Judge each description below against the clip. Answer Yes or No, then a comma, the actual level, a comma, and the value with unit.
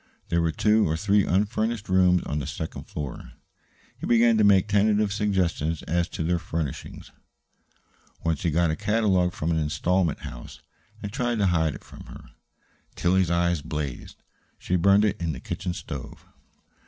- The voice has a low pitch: Yes, very low, 90 Hz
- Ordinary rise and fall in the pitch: Yes, average, 4.1 semitones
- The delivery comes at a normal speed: Yes, average, 165 wpm